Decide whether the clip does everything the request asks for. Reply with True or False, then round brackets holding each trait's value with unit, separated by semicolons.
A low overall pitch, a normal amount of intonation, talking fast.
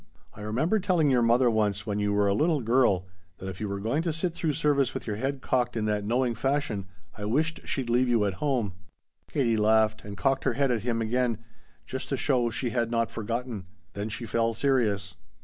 True (115 Hz; 4.1 semitones; 220 wpm)